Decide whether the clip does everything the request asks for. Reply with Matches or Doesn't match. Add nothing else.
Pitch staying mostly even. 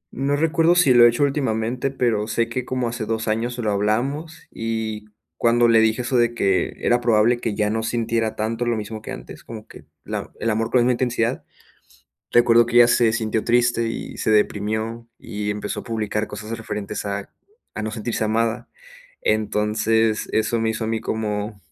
Matches